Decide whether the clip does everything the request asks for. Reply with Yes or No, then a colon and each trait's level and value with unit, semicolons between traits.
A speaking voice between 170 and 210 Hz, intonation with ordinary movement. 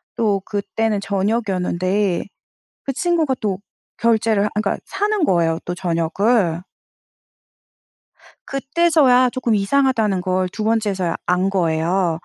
Yes: high, 205 Hz; average, 4.8 semitones